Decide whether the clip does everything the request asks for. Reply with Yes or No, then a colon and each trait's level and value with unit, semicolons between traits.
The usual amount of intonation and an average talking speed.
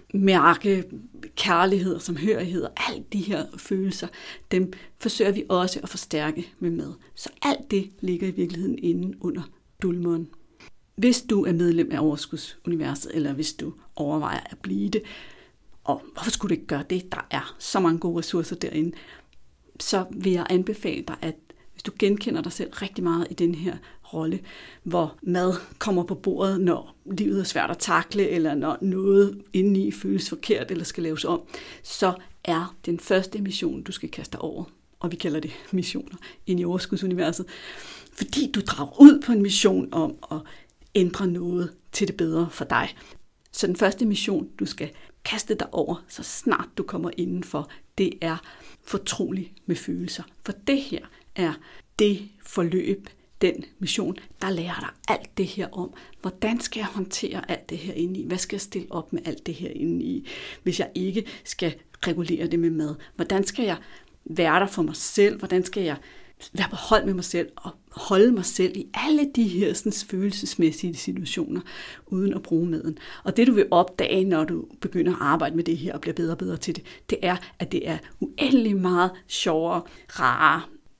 Yes: average, 3.1 semitones; average, 185 wpm